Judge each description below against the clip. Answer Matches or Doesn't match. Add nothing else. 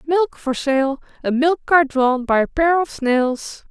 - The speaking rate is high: Doesn't match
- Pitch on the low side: Doesn't match